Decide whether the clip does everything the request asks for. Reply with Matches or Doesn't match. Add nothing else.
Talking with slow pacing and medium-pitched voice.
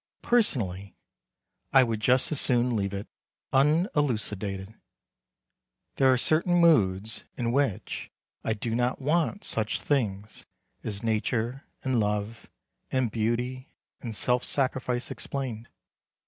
Doesn't match